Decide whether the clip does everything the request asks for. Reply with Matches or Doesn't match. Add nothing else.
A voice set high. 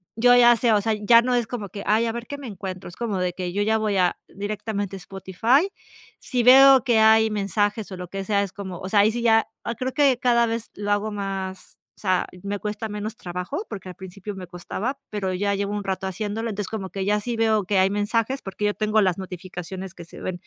Matches